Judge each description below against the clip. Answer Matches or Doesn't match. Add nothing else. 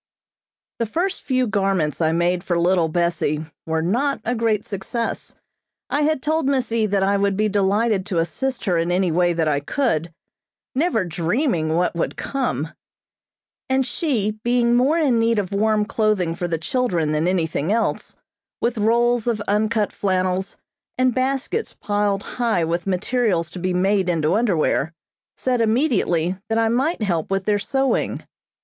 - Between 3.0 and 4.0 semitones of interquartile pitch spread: Doesn't match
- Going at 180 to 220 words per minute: Doesn't match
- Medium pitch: Doesn't match